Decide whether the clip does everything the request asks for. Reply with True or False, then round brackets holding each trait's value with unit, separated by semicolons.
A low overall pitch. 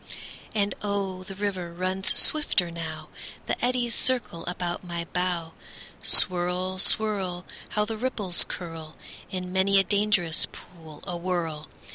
False (185 Hz)